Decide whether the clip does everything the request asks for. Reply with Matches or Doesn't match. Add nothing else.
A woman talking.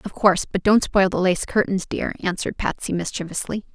Matches